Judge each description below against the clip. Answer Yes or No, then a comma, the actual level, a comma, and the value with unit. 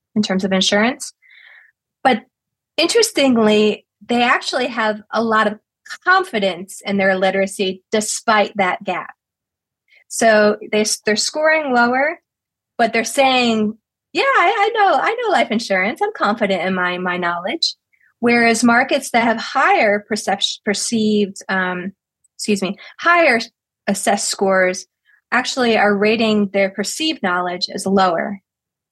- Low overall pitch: No, high, 215 Hz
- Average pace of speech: No, slow, 130 wpm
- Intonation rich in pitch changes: No, average, 4.5 semitones